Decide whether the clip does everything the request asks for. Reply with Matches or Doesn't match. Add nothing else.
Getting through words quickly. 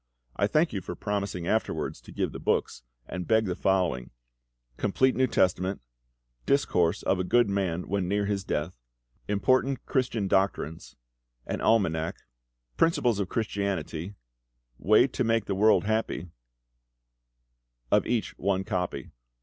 Doesn't match